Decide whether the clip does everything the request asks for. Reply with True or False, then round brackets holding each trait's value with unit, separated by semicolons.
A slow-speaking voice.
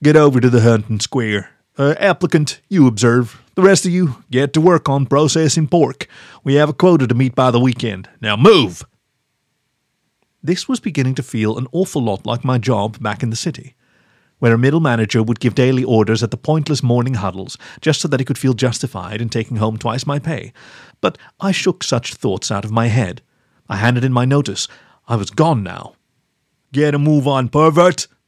False (200 wpm)